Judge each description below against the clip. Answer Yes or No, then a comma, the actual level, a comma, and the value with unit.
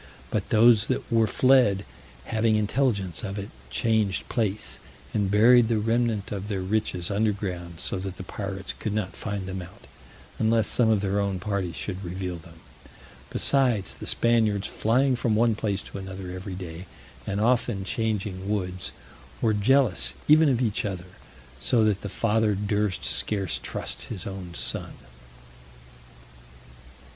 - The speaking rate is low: No, average, 150 wpm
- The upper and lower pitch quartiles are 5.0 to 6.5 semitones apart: No, average, 2.9 semitones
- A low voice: Yes, low, 105 Hz